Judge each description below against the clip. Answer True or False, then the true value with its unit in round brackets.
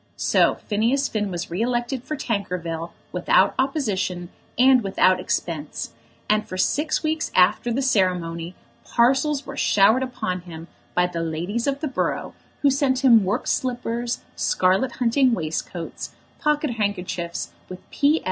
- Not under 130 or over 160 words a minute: True (140 wpm)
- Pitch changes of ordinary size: False (6.5 semitones)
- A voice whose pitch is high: True (220 Hz)